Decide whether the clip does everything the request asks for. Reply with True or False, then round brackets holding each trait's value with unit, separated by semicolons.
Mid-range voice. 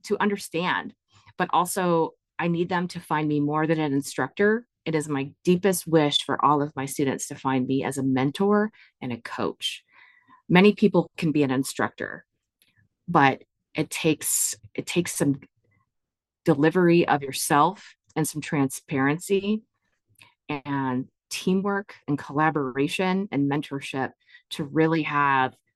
True (150 Hz)